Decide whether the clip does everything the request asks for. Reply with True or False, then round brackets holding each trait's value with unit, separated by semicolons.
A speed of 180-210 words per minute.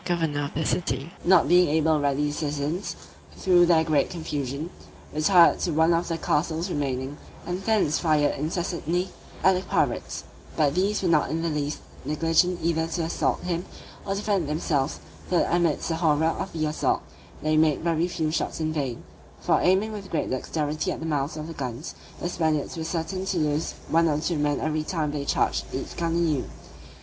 True (195 wpm)